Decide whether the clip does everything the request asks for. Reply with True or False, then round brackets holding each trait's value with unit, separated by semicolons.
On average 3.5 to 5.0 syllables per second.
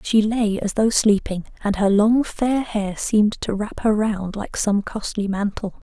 True (4.2 syllables/s)